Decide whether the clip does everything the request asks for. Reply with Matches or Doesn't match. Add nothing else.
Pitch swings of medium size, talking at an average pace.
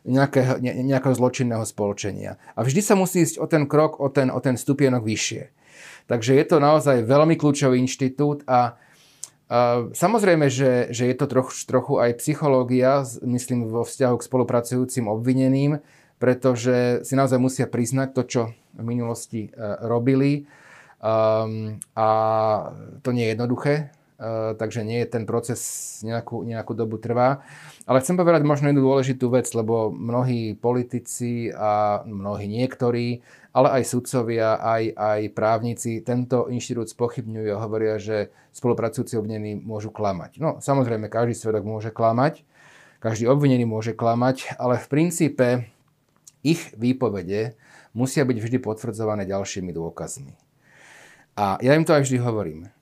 Matches